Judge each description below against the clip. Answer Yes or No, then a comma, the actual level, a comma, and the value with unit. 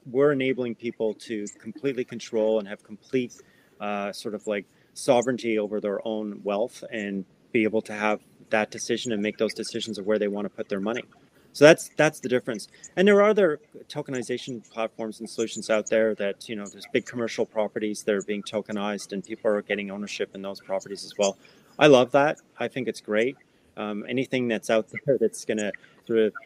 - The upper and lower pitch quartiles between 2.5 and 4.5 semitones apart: Yes, average, 2.9 semitones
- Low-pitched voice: Yes, low, 110 Hz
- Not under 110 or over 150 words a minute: No, fast, 205 wpm